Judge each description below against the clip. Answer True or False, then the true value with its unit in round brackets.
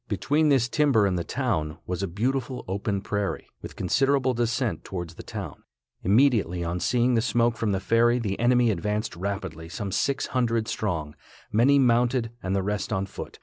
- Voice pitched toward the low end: True (110 Hz)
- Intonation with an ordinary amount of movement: True (4.2 semitones)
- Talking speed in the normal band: True (180 wpm)